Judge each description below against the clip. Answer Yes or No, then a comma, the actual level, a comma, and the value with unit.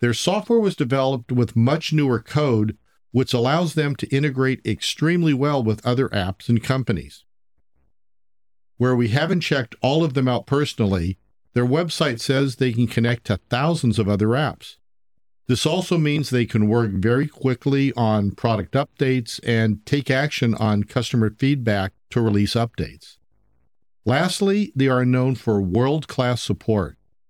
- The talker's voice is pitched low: Yes, low, 120 Hz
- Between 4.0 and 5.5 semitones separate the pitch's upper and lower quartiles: Yes, average, 4.7 semitones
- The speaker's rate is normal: Yes, average, 150 wpm